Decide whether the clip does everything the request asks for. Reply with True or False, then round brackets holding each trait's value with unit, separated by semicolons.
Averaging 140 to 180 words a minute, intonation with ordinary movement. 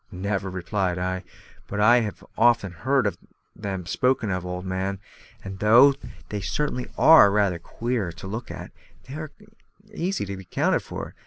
True (150 wpm; 4.4 semitones)